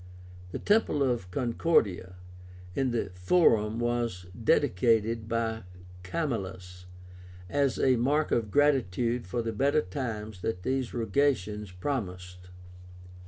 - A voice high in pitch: No, low, 115 Hz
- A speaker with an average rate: No, slow, 110 wpm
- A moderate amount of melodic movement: No, wide, 6.0 semitones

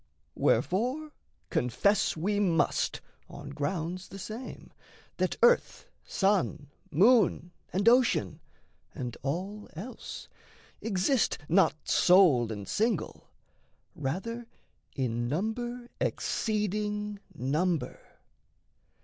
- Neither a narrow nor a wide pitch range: No, wide, 6.3 semitones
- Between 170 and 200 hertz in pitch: Yes, high, 190 Hz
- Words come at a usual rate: No, slow, 85 wpm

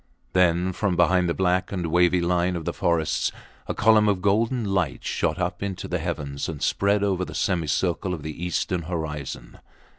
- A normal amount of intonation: No, narrow, 2.1 semitones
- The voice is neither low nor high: No, very low, 90 Hz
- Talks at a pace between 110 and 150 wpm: No, average, 180 wpm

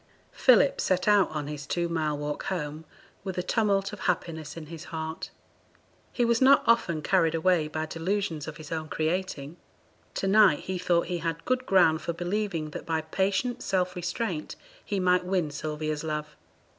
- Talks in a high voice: No, medium, 170 Hz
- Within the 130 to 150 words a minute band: No, average, 175 wpm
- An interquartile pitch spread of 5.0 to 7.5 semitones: No, average, 3.5 semitones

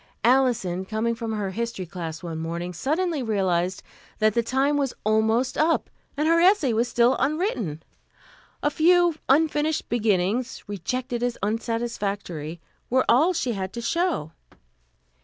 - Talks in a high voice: Yes, high, 235 Hz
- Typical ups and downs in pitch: No, wide, 6.1 semitones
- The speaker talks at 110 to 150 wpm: Yes, average, 140 wpm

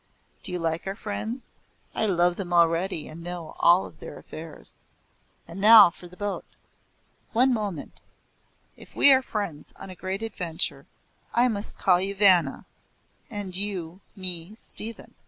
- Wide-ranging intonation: No, average, 3.4 semitones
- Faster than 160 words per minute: No, average, 150 wpm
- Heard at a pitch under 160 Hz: No, medium, 185 Hz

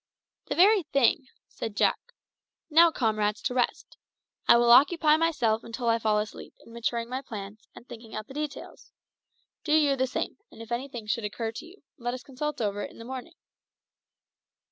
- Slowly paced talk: No, average, 185 wpm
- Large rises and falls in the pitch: No, average, 4.3 semitones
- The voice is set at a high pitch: Yes, high, 240 Hz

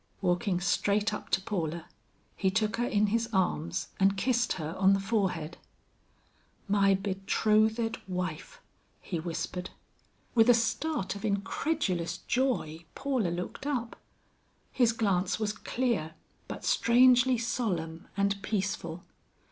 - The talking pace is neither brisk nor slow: No, slow, 125 wpm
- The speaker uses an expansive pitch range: No, average, 4.2 semitones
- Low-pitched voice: No, high, 200 Hz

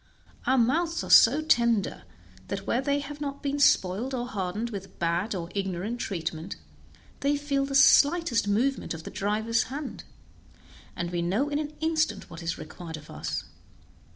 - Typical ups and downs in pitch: No, wide, 7.2 semitones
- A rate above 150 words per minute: Yes, average, 165 wpm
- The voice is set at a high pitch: Yes, high, 235 Hz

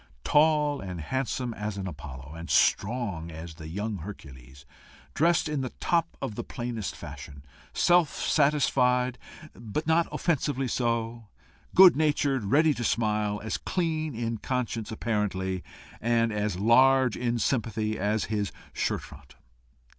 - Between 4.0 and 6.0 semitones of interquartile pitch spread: Yes, wide, 5.4 semitones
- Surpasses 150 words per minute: No, slow, 135 wpm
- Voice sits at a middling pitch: No, low, 115 Hz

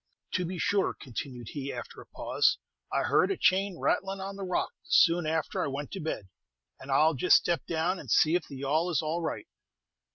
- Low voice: No, medium, 165 Hz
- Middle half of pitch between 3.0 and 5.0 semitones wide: Yes, average, 4.4 semitones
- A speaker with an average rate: No, fast, 215 wpm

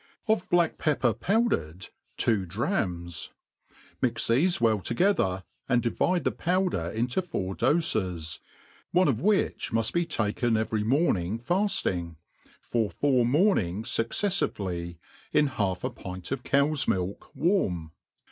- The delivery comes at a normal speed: No, slow, 125 wpm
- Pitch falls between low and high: No, low, 115 Hz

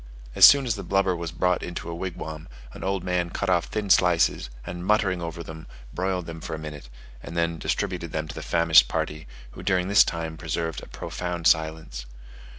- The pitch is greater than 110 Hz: No, very low, 85 Hz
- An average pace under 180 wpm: No, average, 195 wpm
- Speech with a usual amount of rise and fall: No, narrow, 2.3 semitones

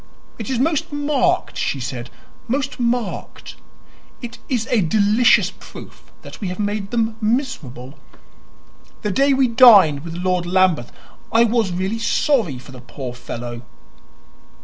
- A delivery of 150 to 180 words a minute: No, average, 140 wpm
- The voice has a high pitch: Yes, high, 210 Hz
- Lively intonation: Yes, wide, 6.9 semitones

